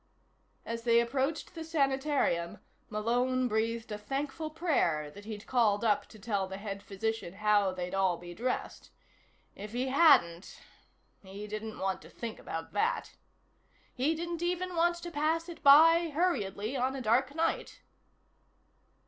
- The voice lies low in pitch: No, high, 235 Hz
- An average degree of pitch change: No, wide, 6.9 semitones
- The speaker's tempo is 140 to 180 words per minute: Yes, average, 150 wpm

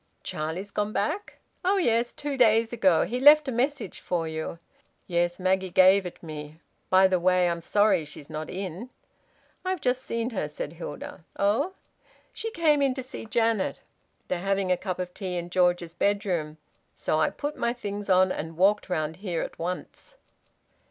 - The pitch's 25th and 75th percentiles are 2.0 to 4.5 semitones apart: No, average, 5.3 semitones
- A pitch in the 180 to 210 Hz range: Yes, high, 190 Hz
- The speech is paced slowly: No, average, 175 wpm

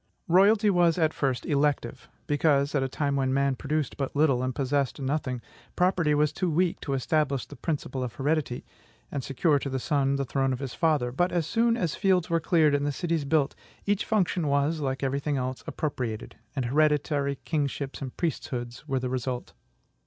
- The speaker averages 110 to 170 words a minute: No, average, 190 wpm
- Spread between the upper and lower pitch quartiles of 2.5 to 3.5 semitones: Yes, average, 3.1 semitones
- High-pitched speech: No, medium, 145 Hz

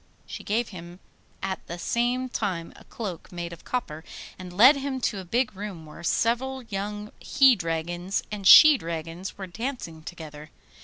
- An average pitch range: No, wide, 5.9 semitones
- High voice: Yes, high, 195 Hz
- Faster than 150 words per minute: Yes, average, 165 wpm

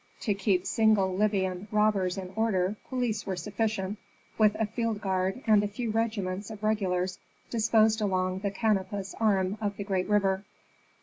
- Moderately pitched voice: No, high, 205 Hz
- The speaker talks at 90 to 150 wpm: No, average, 160 wpm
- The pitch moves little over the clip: Yes, narrow, 2.3 semitones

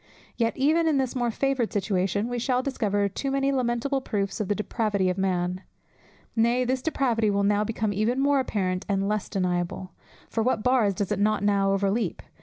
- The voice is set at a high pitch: Yes, high, 215 Hz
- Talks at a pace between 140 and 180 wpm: No, average, 190 wpm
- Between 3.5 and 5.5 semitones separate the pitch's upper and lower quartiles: Yes, average, 4.2 semitones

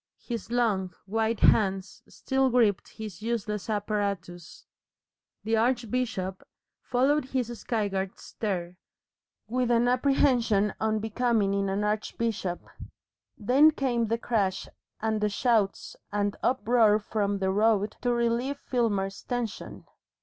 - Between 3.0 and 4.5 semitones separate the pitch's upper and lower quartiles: Yes, average, 3.3 semitones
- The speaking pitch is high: Yes, high, 220 Hz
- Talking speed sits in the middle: No, slow, 115 wpm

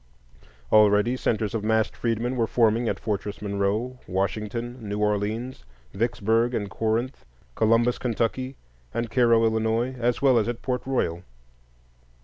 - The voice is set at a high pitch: No, low, 115 Hz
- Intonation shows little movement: Yes, narrow, 2.3 semitones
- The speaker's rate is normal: No, slow, 130 wpm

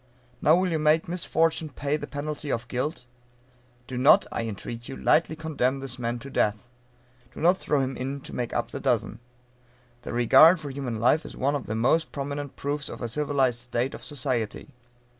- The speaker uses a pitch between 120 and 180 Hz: Yes, medium, 140 Hz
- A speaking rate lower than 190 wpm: No, average, 195 wpm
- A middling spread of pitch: Yes, average, 3.8 semitones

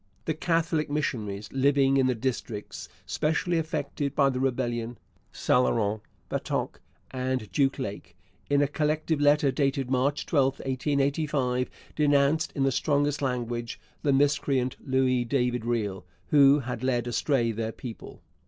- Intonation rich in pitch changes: No, average, 2.9 semitones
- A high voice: No, low, 135 Hz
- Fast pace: No, slow, 135 wpm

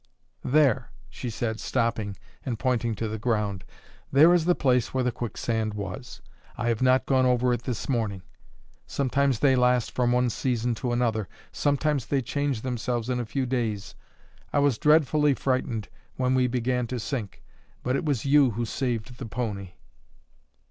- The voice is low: Yes, low, 125 Hz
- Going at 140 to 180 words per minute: Yes, average, 170 wpm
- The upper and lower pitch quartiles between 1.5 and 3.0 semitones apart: Yes, average, 2.7 semitones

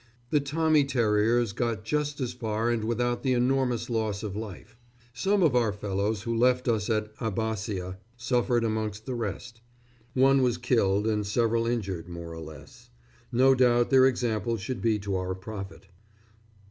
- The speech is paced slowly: No, average, 160 wpm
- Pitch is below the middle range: Yes, low, 115 Hz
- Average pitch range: Yes, average, 3.0 semitones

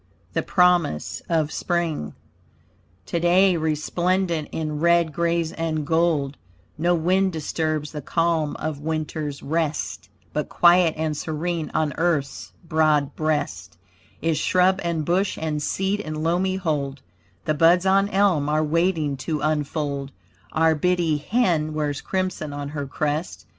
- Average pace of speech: No, slow, 130 wpm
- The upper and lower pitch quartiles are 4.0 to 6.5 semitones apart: No, narrow, 2.4 semitones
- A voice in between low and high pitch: Yes, medium, 160 Hz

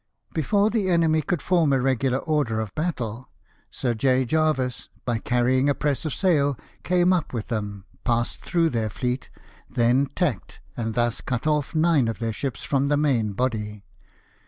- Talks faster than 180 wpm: No, average, 170 wpm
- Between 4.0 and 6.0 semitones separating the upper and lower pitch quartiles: Yes, average, 4.9 semitones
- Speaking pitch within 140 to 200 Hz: No, low, 130 Hz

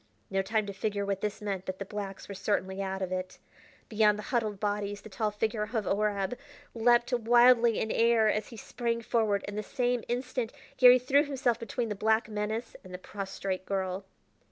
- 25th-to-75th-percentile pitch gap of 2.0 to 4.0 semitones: Yes, average, 2.9 semitones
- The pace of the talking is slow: No, average, 200 wpm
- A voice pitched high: Yes, high, 210 Hz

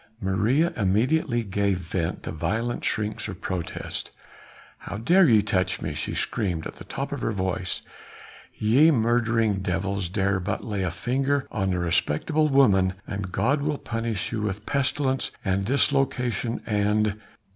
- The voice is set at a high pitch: No, low, 105 Hz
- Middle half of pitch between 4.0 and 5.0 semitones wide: Yes, average, 4.5 semitones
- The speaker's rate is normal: Yes, average, 150 wpm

